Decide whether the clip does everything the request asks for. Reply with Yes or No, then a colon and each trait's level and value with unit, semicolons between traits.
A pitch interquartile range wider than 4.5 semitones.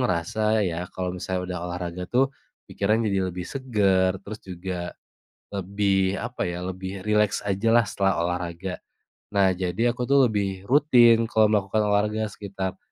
No: average, 2.8 semitones